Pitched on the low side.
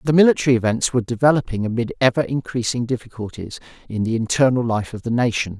Yes: low, 120 Hz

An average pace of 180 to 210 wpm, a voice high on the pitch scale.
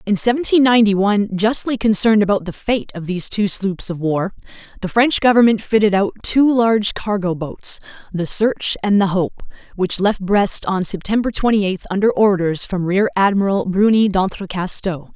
No: average, 170 wpm; high, 200 Hz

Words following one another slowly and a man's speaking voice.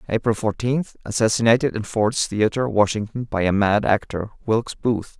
No: average, 150 wpm; male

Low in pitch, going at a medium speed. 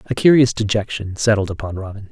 Yes: low, 105 Hz; average, 170 wpm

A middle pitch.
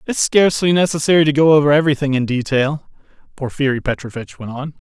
Yes: medium, 145 Hz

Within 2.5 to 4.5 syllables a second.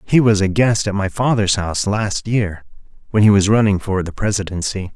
No: 5.3 syllables/s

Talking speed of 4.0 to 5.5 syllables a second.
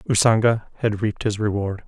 No: 5.7 syllables/s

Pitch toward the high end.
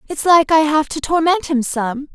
Yes: very high, 295 Hz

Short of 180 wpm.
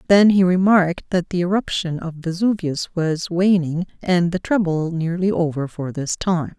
Yes: average, 165 wpm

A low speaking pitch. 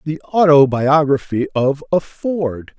No: medium, 145 Hz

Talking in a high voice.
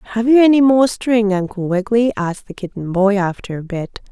Yes: high, 210 Hz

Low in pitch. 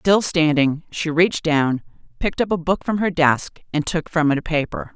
No: medium, 160 Hz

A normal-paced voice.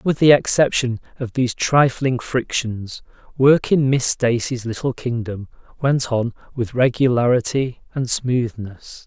No: slow, 125 wpm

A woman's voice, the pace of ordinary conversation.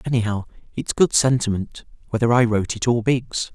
No: male; average, 170 wpm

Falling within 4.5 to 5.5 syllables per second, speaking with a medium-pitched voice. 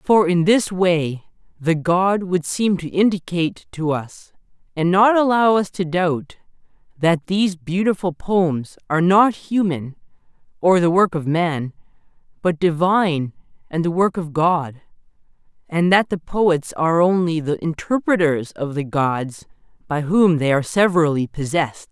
No: 4.3 syllables/s; medium, 170 Hz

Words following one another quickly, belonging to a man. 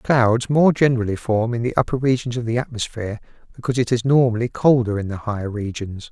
No: average, 195 wpm; male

